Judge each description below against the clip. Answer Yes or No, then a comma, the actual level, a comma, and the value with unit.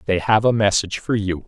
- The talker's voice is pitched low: Yes, low, 100 Hz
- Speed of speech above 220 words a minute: Yes, fast, 245 wpm